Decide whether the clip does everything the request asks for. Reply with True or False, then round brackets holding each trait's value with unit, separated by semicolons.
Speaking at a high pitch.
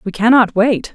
True (220 Hz)